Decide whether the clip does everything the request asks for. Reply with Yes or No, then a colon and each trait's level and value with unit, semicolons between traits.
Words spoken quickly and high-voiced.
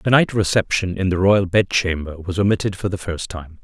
No: fast, 215 wpm; very low, 95 Hz